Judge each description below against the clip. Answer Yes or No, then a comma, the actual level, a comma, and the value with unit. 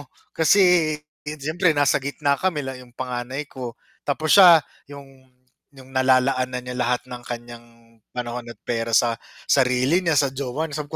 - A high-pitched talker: No, low, 130 Hz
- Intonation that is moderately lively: Yes, average, 3.1 semitones